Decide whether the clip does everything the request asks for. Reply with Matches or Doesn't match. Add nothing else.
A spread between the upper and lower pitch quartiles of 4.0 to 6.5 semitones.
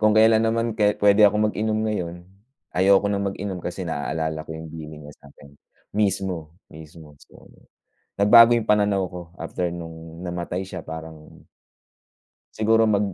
Matches